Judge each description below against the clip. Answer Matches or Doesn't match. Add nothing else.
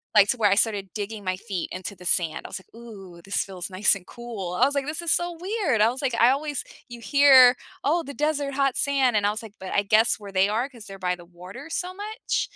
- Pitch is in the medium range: Doesn't match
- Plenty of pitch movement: Matches